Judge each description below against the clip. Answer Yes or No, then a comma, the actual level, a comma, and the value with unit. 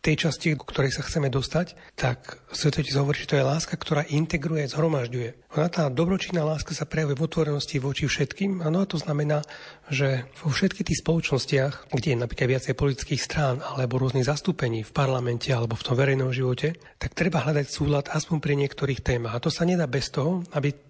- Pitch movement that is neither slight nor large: Yes, average, 3.1 semitones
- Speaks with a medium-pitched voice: Yes, medium, 145 Hz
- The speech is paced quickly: Yes, fast, 195 wpm